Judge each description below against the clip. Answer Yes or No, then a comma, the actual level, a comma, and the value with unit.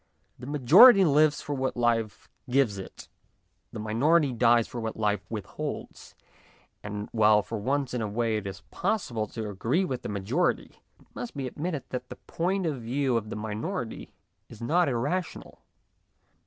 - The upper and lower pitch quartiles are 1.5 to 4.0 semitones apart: No, average, 5.3 semitones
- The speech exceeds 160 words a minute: Yes, average, 170 wpm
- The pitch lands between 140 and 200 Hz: No, low, 120 Hz